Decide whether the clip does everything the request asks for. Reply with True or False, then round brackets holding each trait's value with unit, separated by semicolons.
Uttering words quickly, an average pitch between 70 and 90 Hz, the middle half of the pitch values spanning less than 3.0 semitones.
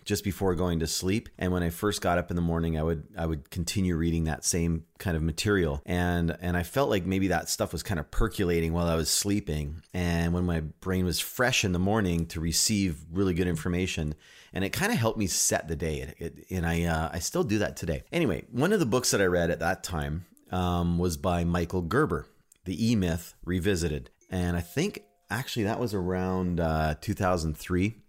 True (220 wpm; 85 Hz; 2.4 semitones)